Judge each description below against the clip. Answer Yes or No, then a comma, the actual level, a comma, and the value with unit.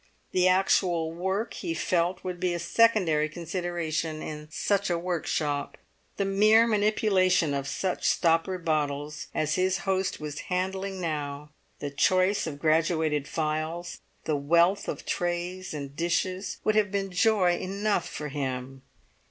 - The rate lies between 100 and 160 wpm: Yes, average, 140 wpm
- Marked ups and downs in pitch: No, average, 3.5 semitones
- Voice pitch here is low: No, medium, 175 Hz